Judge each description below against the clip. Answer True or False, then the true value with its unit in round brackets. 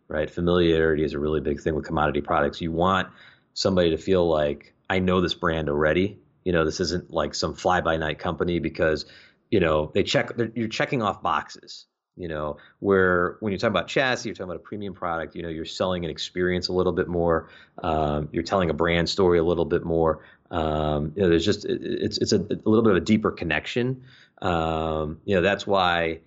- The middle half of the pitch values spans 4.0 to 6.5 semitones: False (2.8 semitones)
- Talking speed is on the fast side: True (215 wpm)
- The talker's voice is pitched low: True (85 Hz)